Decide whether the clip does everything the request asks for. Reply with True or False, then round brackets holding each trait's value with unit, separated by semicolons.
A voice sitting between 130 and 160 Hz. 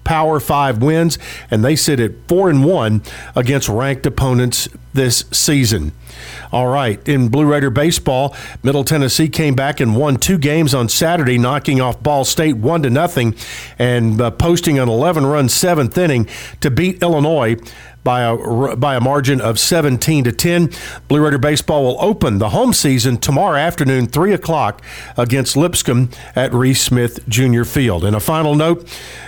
True (135 Hz)